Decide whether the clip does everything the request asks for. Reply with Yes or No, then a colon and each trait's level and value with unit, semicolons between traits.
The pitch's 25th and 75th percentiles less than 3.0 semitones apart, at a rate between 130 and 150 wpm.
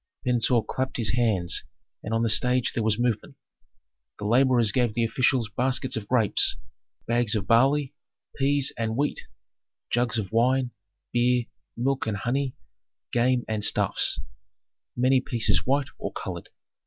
Yes: narrow, 2.5 semitones; average, 140 wpm